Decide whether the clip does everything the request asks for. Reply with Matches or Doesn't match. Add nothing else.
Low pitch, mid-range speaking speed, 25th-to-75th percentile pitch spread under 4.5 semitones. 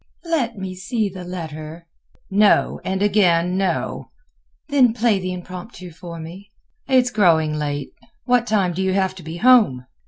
Doesn't match